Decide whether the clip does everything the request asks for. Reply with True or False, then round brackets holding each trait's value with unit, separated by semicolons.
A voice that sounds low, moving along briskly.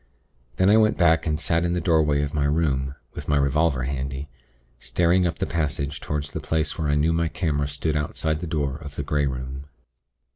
True (75 Hz; 210 wpm)